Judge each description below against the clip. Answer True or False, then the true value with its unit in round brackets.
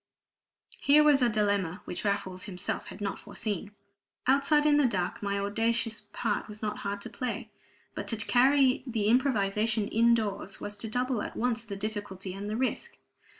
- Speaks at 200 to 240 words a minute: False (175 wpm)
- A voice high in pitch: True (215 Hz)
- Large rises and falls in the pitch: False (3.5 semitones)